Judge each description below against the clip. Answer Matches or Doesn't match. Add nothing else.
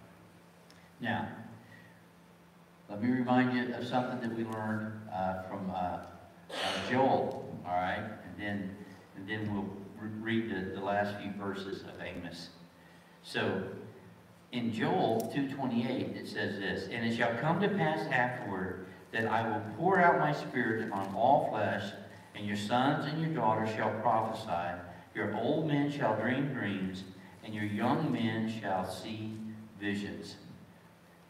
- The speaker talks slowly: Doesn't match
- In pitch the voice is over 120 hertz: Doesn't match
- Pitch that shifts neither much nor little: Matches